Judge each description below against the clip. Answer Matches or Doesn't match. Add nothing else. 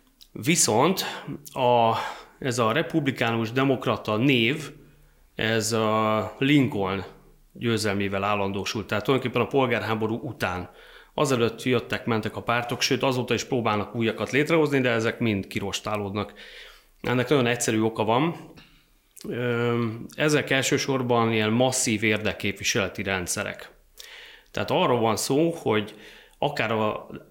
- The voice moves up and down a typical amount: Matches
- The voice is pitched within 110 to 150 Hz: Matches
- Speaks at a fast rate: Doesn't match